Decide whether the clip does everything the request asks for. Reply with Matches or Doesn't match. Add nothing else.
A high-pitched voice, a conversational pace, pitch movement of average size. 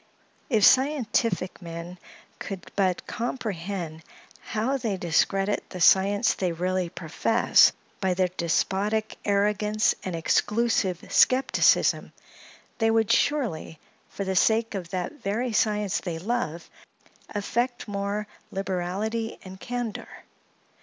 Doesn't match